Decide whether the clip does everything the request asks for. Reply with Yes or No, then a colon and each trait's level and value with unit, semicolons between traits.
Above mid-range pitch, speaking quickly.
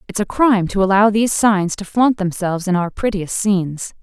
Yes: high, 200 Hz; fast, 210 wpm